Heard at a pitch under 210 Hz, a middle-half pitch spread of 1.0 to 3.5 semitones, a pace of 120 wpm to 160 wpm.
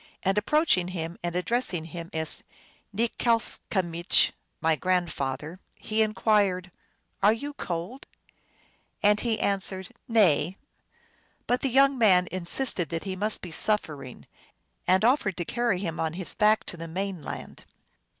No: high, 190 Hz; average, 4.3 semitones; average, 150 wpm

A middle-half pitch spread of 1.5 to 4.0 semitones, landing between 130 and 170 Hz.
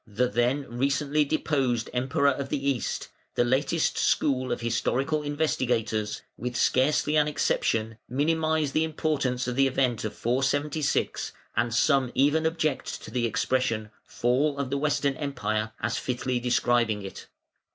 Yes: average, 3.2 semitones; low, 135 Hz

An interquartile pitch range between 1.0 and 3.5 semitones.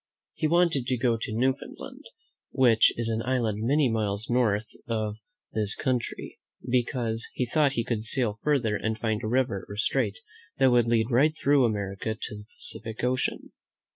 Yes: average, 2.9 semitones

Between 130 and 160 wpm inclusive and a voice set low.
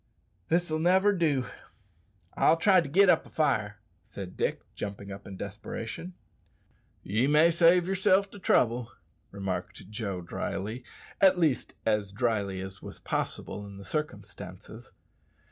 Yes: slow, 135 wpm; low, 120 Hz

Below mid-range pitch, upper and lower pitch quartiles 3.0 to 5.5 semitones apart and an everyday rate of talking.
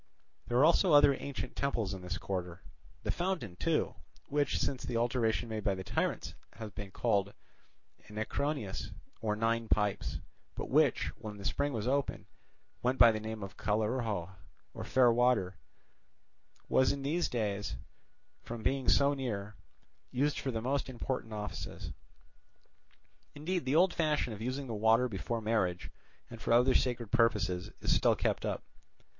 Yes: low, 115 Hz; average, 4.2 semitones; average, 155 wpm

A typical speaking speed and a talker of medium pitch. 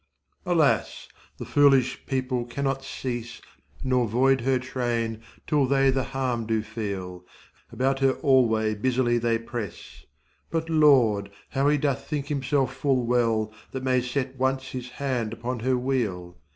No: average, 145 wpm; low, 130 Hz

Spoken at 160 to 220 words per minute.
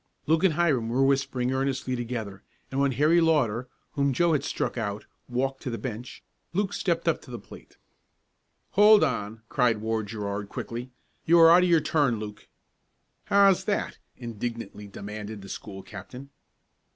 Yes: average, 165 wpm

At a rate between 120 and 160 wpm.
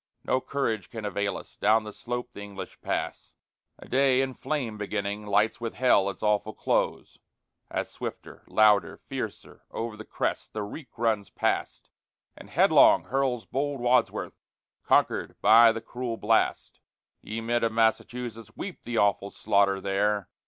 Yes: average, 150 wpm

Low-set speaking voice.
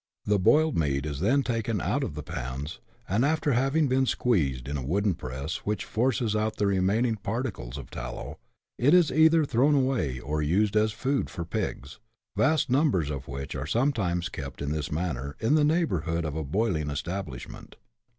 Yes: low, 100 Hz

